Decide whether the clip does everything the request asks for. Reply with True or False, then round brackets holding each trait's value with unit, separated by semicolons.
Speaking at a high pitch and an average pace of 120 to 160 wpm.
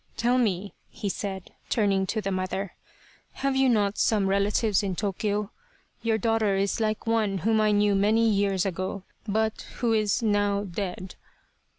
False (205 Hz; 170 wpm)